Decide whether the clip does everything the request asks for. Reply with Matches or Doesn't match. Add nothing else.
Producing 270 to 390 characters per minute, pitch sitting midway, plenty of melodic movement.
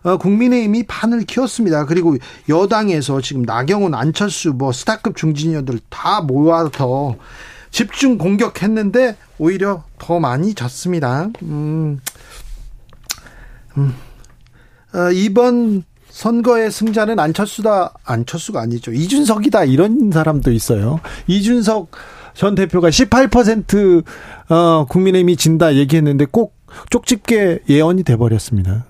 Doesn't match